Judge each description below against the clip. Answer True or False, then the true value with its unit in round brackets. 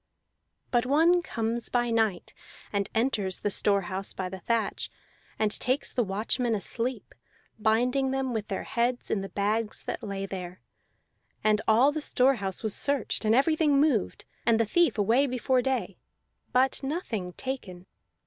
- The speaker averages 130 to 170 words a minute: True (160 wpm)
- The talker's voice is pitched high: True (230 Hz)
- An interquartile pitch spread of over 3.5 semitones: True (4.5 semitones)